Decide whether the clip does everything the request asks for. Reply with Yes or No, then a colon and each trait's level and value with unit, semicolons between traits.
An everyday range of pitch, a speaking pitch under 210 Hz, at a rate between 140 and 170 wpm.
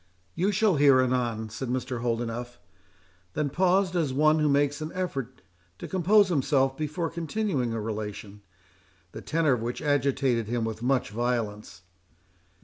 Yes: average, 4.9 semitones; low, 135 Hz; average, 145 wpm